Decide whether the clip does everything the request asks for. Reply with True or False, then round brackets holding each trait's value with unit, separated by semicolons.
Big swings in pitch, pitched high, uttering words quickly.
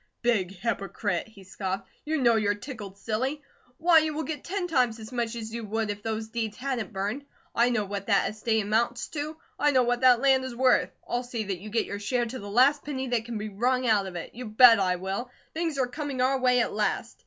False (3.7 semitones; 235 Hz; 235 wpm)